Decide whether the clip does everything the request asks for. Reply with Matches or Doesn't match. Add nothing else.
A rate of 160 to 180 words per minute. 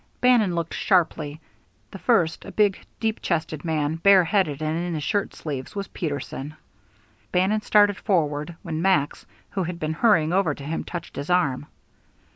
Matches